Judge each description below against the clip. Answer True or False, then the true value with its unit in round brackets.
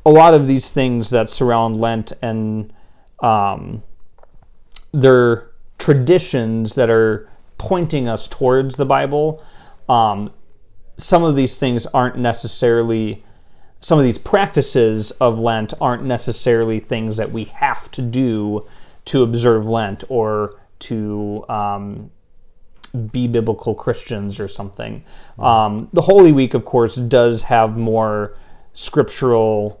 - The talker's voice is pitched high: False (115 Hz)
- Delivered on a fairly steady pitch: False (3.3 semitones)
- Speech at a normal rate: False (125 wpm)